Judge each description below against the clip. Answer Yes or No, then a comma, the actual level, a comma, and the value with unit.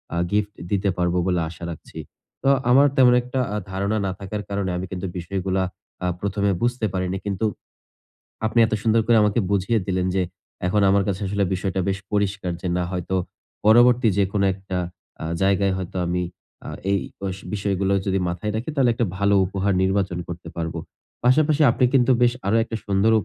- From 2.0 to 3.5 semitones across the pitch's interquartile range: Yes, average, 2.7 semitones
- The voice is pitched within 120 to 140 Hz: No, low, 100 Hz